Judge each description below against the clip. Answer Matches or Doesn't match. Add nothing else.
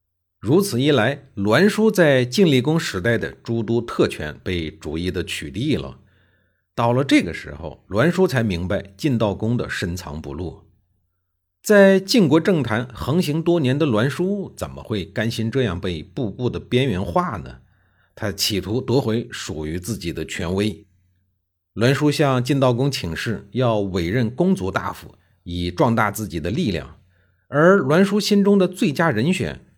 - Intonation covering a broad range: Matches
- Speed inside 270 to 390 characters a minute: Doesn't match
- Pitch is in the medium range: Doesn't match